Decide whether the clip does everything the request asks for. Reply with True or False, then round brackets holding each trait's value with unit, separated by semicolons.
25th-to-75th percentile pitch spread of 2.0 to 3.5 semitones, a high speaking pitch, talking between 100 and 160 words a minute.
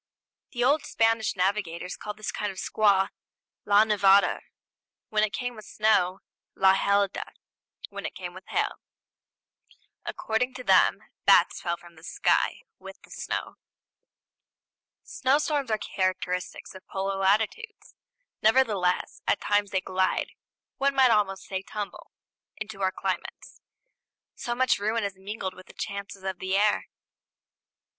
True (2.6 semitones; 205 Hz; 140 wpm)